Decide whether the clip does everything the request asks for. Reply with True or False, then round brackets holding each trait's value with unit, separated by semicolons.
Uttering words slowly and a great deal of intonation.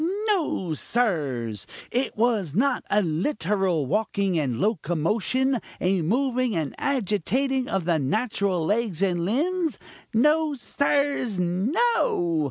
True (110 wpm; 7.4 semitones)